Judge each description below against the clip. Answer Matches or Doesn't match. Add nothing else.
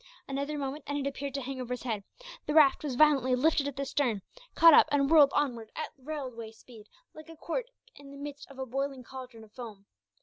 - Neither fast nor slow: Doesn't match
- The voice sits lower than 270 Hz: Doesn't match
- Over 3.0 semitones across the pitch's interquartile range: Doesn't match